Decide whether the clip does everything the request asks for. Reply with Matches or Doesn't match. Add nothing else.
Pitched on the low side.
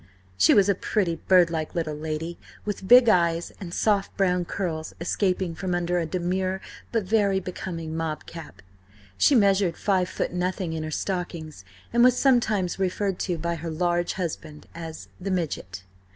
Doesn't match